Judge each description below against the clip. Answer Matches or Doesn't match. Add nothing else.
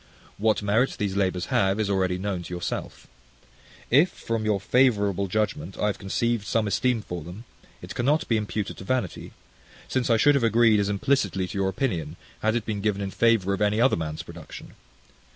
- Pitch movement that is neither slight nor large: Matches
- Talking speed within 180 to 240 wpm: Matches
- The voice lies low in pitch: Matches